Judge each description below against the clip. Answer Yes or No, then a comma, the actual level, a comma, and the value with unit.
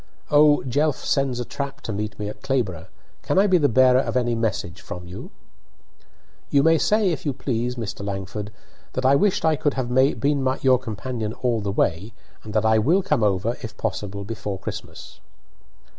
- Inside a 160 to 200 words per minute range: Yes, average, 190 wpm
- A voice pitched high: No, low, 120 Hz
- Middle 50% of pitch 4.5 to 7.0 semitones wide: Yes, average, 4.8 semitones